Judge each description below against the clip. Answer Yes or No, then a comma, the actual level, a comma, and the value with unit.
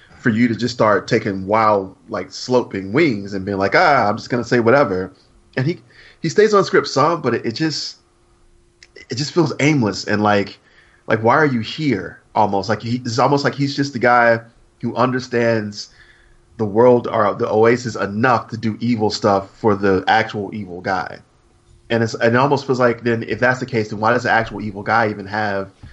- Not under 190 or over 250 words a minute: Yes, fast, 205 wpm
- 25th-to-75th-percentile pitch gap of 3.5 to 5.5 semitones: No, average, 3.0 semitones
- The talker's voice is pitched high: No, low, 115 Hz